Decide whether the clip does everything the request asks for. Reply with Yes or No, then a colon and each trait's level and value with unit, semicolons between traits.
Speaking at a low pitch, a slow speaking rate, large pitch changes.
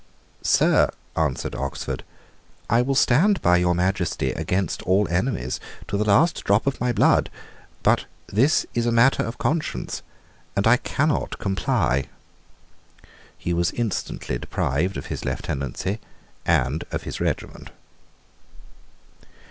Yes: low, 100 Hz; slow, 125 wpm; wide, 5.9 semitones